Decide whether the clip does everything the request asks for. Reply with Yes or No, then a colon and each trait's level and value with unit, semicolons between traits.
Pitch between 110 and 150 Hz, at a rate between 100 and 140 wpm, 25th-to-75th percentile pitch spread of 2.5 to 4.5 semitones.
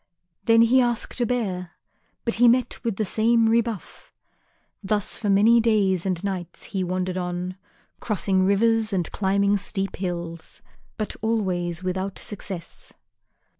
No: high, 200 Hz; slow, 135 wpm; average, 3.6 semitones